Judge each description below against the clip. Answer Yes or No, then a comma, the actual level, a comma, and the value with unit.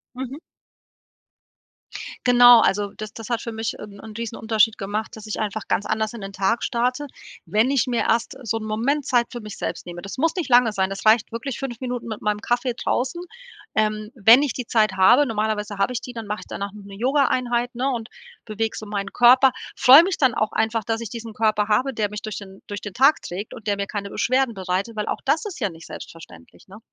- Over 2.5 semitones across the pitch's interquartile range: Yes, average, 2.9 semitones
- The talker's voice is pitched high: Yes, high, 225 Hz